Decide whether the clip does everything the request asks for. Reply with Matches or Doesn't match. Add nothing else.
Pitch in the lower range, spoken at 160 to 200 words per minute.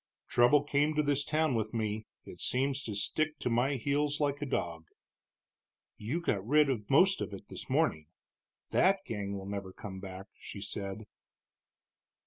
Matches